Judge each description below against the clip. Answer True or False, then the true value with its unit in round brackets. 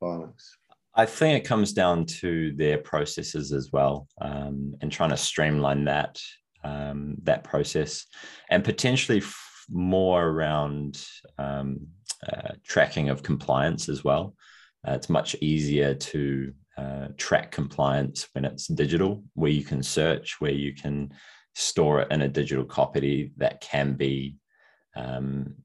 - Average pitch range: False (2.3 semitones)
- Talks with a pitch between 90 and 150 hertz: False (70 Hz)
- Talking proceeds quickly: False (140 wpm)